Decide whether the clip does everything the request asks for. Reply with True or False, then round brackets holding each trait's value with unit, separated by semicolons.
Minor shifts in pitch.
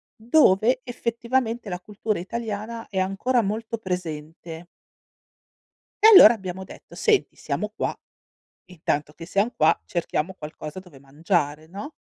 False (5.6 semitones)